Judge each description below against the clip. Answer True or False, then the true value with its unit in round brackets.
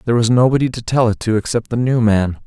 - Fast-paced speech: True (270 wpm)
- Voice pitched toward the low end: True (115 Hz)